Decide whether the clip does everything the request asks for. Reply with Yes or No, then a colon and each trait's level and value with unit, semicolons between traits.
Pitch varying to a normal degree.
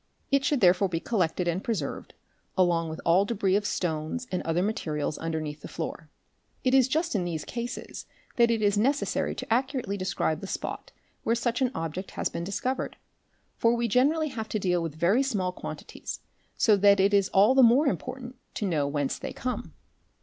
No: wide, 6.1 semitones